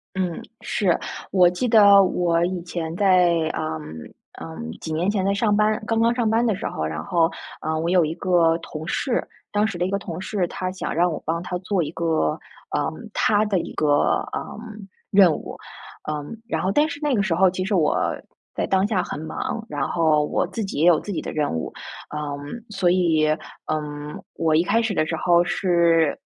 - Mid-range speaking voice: Yes, medium, 180 Hz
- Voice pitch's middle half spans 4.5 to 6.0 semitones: No, average, 3.7 semitones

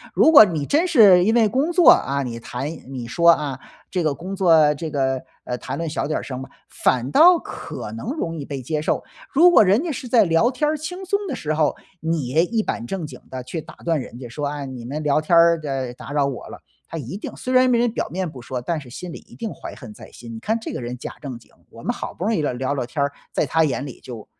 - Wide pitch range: Yes, wide, 8.2 semitones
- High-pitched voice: No, medium, 155 Hz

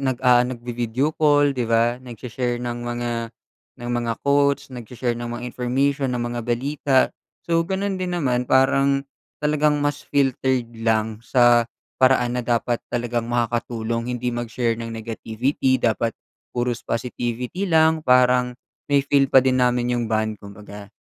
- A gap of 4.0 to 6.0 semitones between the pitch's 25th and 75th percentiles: No, narrow, 2.5 semitones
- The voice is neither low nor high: No, low, 125 Hz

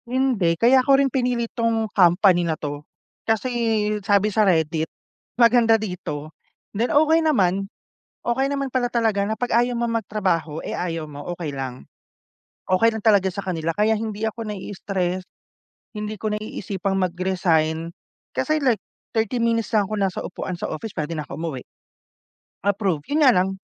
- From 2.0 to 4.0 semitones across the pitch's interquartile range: No, average, 4.8 semitones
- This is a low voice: No, high, 205 Hz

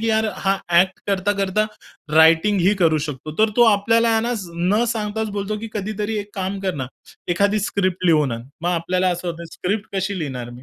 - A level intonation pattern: No, average, 3.7 semitones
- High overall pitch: Yes, high, 195 Hz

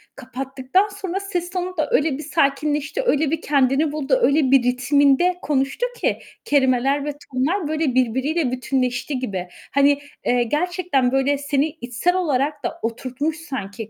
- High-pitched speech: Yes, very high, 280 Hz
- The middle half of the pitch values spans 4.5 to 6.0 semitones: No, average, 3.6 semitones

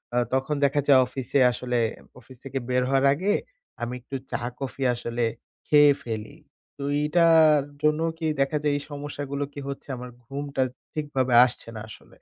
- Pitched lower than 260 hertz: Yes, medium, 140 Hz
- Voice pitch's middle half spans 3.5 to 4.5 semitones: No, average, 2.7 semitones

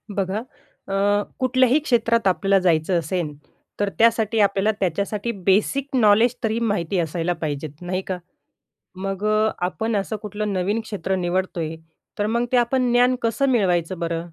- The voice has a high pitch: Yes, high, 200 Hz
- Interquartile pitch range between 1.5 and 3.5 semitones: No, average, 4.0 semitones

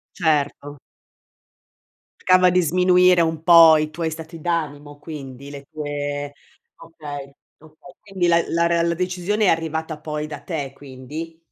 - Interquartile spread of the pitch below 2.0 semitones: No, average, 2.7 semitones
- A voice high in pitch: No, medium, 160 Hz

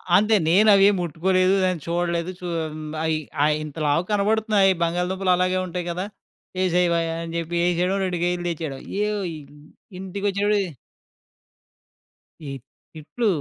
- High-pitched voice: No, medium, 180 Hz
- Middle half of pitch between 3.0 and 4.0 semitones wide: No, narrow, 2.6 semitones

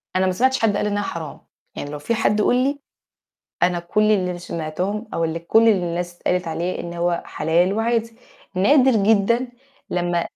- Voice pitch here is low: No, medium, 185 Hz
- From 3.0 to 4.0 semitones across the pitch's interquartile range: No, average, 4.5 semitones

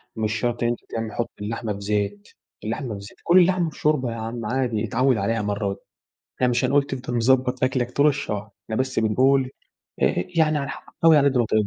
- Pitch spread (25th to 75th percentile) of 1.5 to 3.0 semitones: No, average, 3.8 semitones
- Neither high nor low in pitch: No, low, 120 Hz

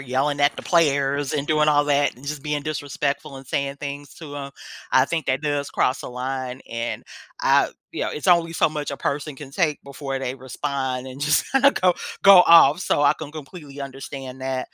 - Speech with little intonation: Yes, narrow, 2.1 semitones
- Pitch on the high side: No, medium, 140 Hz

